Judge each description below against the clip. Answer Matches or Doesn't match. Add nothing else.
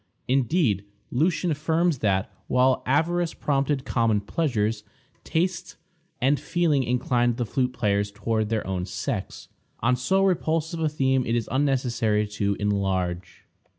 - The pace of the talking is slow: Matches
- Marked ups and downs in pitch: Matches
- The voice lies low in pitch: Matches